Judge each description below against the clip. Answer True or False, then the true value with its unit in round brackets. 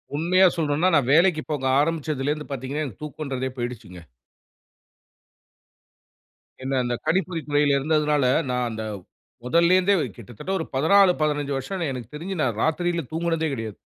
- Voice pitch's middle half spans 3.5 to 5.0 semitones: True (4.0 semitones)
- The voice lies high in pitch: False (150 Hz)